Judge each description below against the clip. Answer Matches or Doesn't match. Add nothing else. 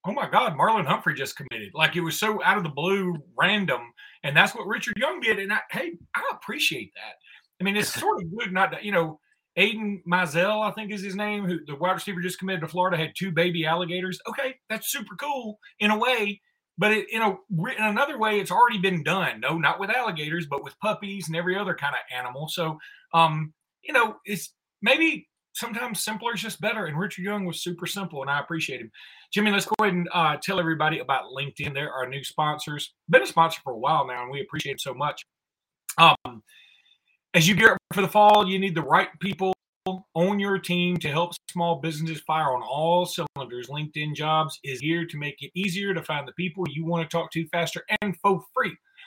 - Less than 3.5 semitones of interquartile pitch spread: Doesn't match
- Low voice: Doesn't match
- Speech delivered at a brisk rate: Matches